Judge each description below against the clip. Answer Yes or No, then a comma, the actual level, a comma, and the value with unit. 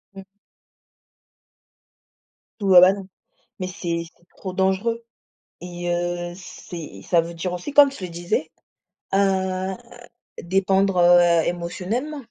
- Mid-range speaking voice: Yes, medium, 180 Hz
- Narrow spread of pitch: Yes, narrow, 1.9 semitones